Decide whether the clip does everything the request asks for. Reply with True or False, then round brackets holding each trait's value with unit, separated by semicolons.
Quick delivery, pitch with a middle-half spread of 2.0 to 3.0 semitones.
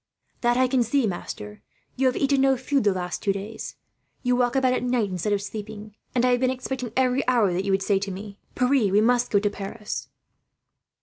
False (225 wpm; 4.0 semitones)